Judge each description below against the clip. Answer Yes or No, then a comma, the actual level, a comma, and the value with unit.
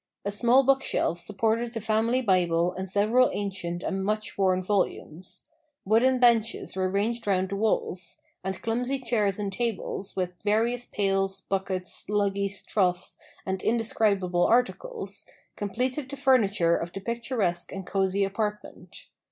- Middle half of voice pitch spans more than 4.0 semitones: No, average, 3.5 semitones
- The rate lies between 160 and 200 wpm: No, slow, 135 wpm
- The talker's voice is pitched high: Yes, high, 205 Hz